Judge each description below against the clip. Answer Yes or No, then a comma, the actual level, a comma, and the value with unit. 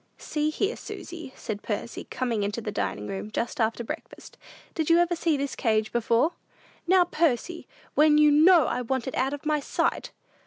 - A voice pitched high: Yes, very high, 275 Hz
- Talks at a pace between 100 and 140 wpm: No, average, 185 wpm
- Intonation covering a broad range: Yes, wide, 5.8 semitones